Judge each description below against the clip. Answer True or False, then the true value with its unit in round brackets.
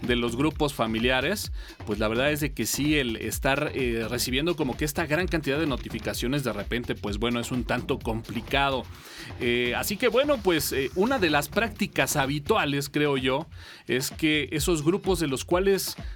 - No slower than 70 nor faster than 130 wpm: False (185 wpm)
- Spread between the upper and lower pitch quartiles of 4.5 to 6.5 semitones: True (4.9 semitones)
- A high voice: False (135 Hz)